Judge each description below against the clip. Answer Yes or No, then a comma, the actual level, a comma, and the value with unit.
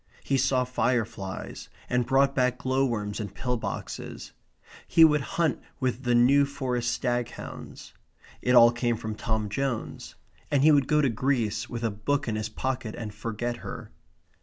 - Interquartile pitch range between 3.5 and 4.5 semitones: No, average, 3.1 semitones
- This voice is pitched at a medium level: No, low, 125 Hz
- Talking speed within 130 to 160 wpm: No, average, 170 wpm